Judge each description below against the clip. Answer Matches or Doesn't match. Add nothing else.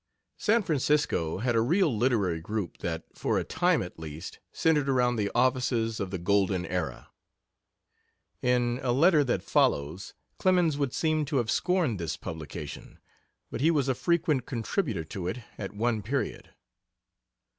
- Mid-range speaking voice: Doesn't match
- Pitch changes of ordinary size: Doesn't match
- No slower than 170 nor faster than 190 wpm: Doesn't match